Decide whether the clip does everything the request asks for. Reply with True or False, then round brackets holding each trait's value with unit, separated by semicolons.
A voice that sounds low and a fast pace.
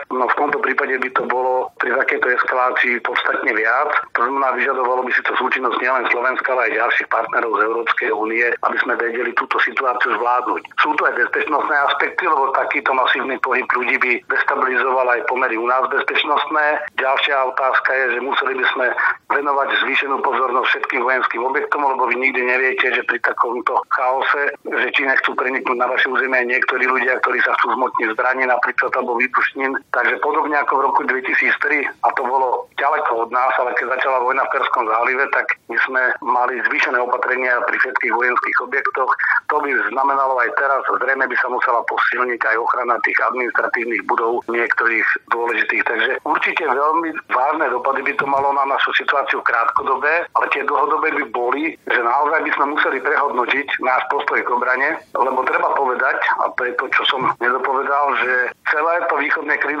False (150 Hz; 180 wpm)